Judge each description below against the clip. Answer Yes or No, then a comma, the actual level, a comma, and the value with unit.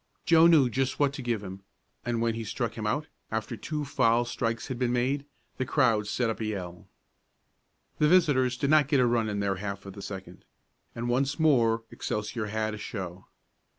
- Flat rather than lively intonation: No, average, 4.2 semitones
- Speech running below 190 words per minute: No, average, 200 wpm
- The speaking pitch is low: Yes, low, 120 Hz